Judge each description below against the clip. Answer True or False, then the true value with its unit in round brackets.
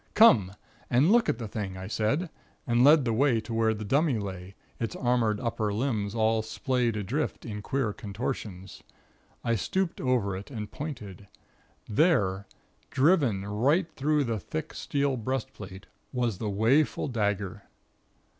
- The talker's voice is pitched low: True (115 Hz)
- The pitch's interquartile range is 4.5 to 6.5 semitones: True (4.8 semitones)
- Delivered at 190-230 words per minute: False (145 wpm)